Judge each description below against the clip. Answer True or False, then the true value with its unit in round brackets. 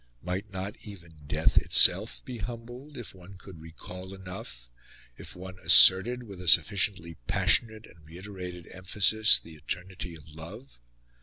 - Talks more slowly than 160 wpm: True (140 wpm)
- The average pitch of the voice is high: False (95 Hz)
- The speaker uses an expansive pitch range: False (3.7 semitones)